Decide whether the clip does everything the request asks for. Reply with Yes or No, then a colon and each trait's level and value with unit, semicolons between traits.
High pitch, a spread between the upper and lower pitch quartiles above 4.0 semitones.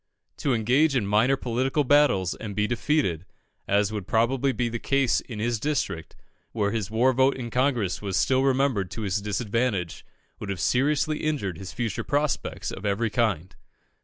No: low, 115 Hz; average, 4.7 semitones